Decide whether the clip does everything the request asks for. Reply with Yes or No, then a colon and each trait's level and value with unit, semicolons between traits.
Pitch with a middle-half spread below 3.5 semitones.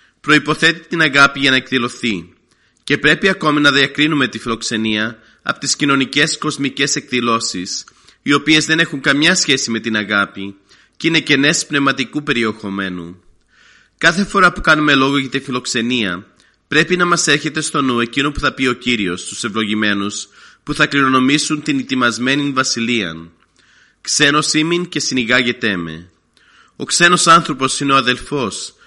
No: average, 5.0 semitones